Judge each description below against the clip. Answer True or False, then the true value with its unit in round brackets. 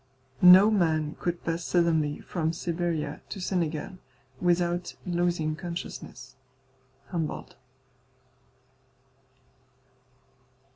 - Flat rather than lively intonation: True (2.0 semitones)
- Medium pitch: True (170 Hz)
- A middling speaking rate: False (70 wpm)